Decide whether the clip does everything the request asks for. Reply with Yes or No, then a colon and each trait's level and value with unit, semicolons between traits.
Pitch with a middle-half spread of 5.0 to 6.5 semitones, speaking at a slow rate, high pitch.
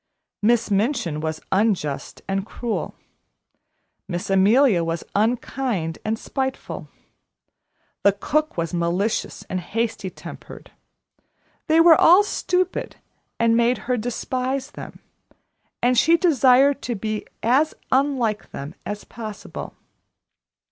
Yes: wide, 5.4 semitones; slow, 110 wpm; high, 230 Hz